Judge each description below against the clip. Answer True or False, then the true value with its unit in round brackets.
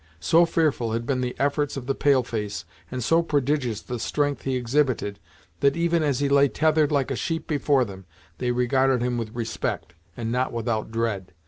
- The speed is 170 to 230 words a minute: True (195 wpm)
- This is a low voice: True (130 Hz)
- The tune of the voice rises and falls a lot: False (3.6 semitones)